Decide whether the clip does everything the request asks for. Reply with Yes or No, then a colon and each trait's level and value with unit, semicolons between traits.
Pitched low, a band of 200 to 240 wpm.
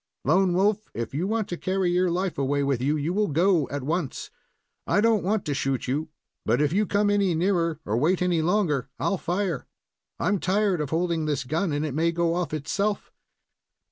No: medium, 170 Hz; fast, 205 wpm